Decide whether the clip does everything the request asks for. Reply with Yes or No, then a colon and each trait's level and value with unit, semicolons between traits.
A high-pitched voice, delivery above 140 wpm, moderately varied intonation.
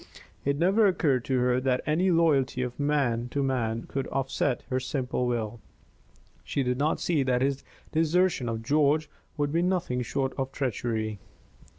No: low, 135 Hz; average, 165 wpm; average, 3.4 semitones